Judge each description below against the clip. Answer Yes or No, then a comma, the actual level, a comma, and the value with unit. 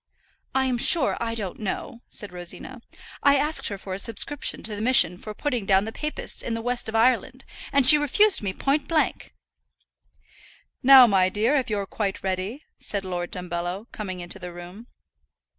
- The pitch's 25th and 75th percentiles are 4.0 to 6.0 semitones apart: Yes, wide, 5.5 semitones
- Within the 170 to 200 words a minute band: Yes, average, 175 wpm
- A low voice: No, high, 220 Hz